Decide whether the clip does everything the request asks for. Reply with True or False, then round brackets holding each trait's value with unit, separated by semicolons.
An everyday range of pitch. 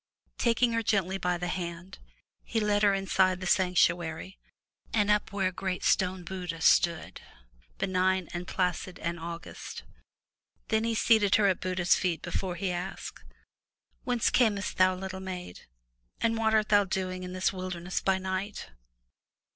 False (2.1 semitones)